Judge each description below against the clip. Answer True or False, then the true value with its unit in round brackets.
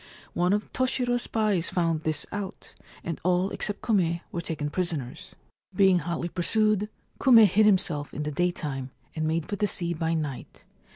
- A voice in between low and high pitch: True (175 Hz)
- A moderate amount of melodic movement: True (4.3 semitones)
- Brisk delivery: False (165 wpm)